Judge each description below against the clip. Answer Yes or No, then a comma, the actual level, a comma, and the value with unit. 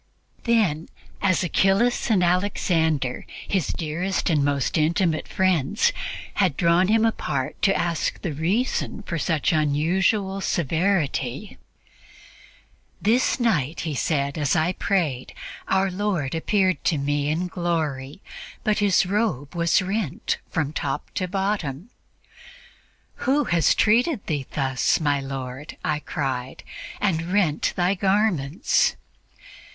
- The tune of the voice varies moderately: Yes, average, 4.9 semitones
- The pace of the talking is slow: Yes, slow, 120 wpm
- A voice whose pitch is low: No, medium, 170 Hz